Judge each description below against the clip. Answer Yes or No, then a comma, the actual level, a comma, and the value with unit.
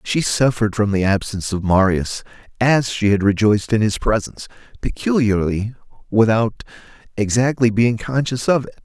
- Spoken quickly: No, average, 145 wpm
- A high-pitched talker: No, low, 110 Hz